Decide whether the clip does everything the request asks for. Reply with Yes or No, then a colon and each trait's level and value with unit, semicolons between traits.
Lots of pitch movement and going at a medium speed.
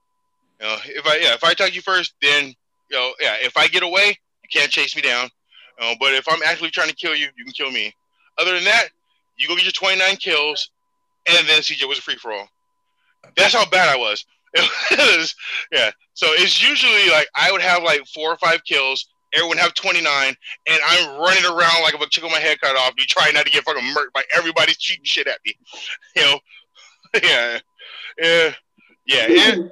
No: wide, 8.8 semitones; fast, 220 wpm